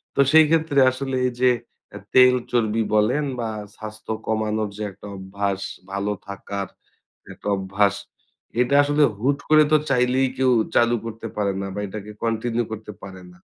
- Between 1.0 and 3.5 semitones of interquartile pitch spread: No, average, 4.1 semitones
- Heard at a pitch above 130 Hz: No, low, 110 Hz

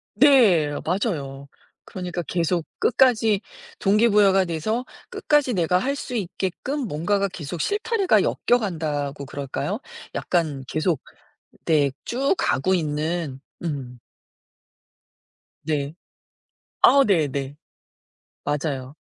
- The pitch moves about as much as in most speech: No, wide, 6.5 semitones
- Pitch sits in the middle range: Yes, medium, 175 Hz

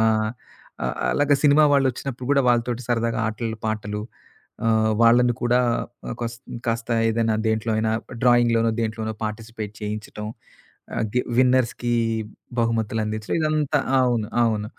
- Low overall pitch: Yes, low, 115 Hz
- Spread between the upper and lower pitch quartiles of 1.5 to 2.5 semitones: Yes, narrow, 2.0 semitones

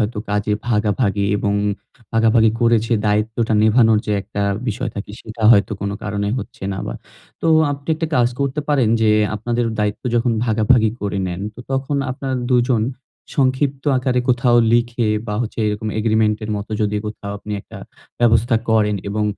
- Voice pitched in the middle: No, low, 110 Hz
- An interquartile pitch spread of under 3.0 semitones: Yes, narrow, 2.6 semitones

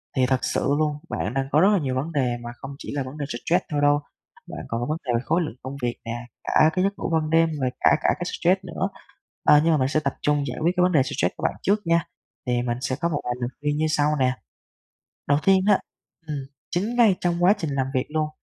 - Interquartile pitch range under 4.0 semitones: No, average, 4.5 semitones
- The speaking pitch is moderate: Yes, medium, 150 Hz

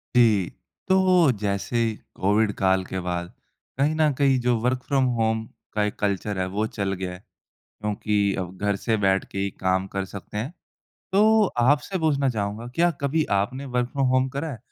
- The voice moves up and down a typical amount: No, wide, 5.8 semitones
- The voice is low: Yes, low, 110 Hz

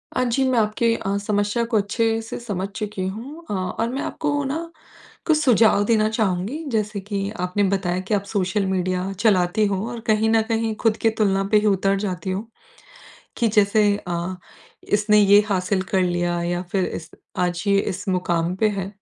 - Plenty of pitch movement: No, average, 3.1 semitones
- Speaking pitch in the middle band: No, high, 205 Hz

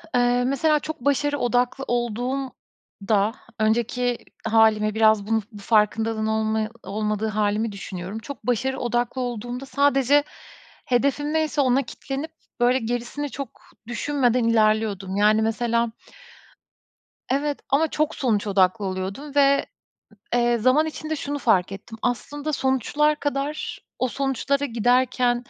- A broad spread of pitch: No, average, 4.1 semitones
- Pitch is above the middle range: Yes, high, 245 Hz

